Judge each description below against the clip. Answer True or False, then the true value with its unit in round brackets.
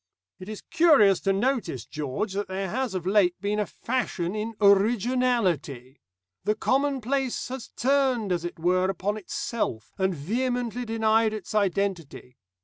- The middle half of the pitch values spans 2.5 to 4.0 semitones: False (4.9 semitones)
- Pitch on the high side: True (210 Hz)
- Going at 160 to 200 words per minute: False (145 wpm)